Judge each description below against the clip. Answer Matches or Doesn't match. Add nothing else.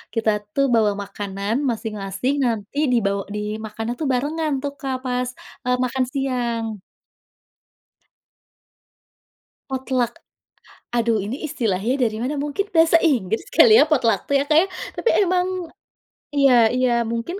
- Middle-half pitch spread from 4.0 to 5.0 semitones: Matches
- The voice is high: Matches